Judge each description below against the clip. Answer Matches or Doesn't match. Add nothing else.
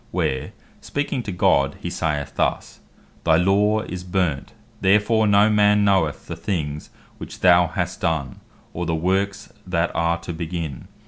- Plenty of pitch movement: Doesn't match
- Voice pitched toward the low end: Matches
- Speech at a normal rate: Matches